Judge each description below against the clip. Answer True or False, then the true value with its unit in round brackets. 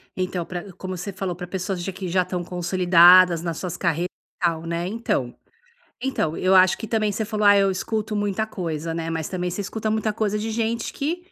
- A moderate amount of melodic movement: True (3.4 semitones)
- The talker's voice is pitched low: False (185 Hz)